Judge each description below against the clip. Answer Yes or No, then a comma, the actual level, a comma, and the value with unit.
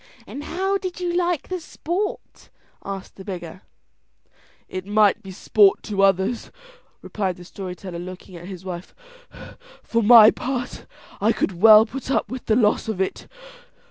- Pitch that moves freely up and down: Yes, wide, 5.7 semitones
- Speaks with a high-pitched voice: Yes, high, 210 Hz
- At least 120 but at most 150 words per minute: No, average, 160 wpm